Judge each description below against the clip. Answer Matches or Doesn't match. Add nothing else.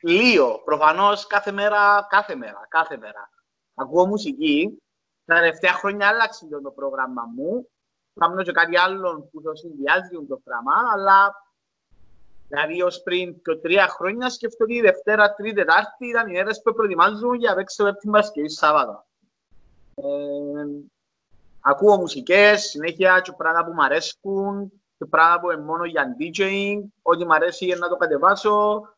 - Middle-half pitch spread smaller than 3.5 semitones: Doesn't match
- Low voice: Doesn't match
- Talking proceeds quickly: Doesn't match